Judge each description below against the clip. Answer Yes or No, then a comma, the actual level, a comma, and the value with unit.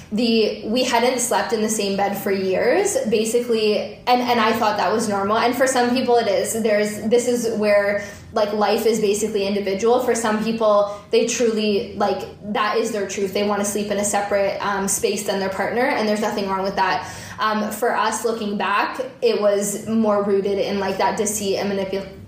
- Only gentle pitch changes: Yes, narrow, 2.2 semitones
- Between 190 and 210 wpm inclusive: Yes, fast, 205 wpm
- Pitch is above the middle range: Yes, high, 210 Hz